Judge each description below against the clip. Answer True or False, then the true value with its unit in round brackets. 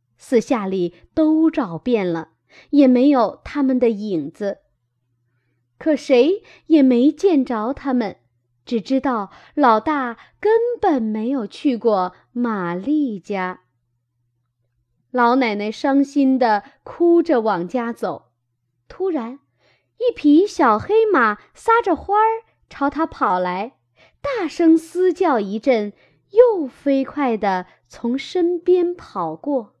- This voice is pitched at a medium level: False (250 Hz)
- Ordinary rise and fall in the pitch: False (8.5 semitones)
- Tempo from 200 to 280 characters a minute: False (155 characters per minute)